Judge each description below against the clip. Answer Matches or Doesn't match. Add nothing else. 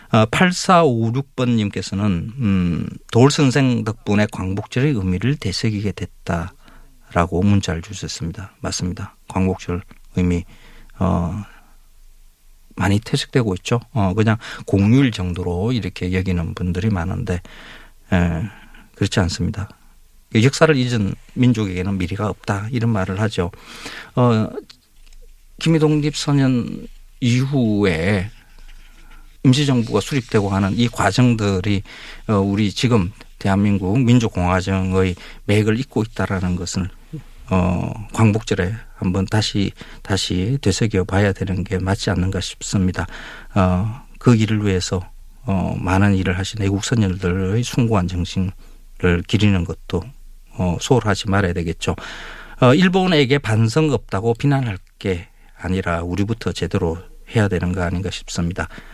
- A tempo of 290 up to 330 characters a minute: Doesn't match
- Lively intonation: Doesn't match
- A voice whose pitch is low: Matches